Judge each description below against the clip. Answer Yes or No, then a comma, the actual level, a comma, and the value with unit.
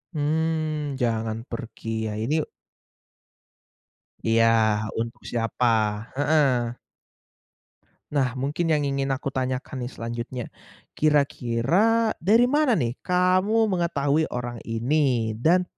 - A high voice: No, medium, 140 Hz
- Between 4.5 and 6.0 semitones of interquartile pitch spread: Yes, average, 5.1 semitones